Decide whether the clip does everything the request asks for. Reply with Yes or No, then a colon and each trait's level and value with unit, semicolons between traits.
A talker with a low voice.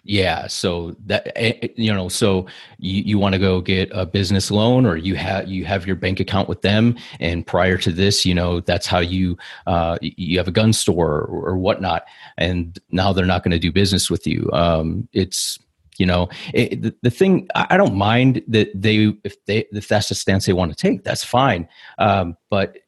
Yes: very low, 95 Hz